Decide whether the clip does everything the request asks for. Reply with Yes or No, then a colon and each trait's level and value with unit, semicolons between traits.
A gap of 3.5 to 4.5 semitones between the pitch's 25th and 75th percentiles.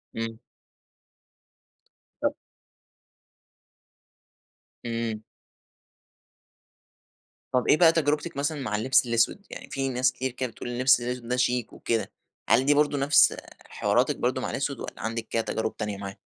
No: average, 3.0 semitones